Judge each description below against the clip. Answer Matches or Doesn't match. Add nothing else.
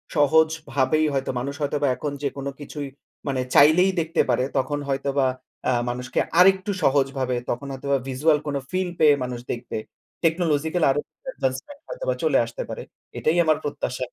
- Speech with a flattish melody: Doesn't match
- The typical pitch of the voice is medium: Matches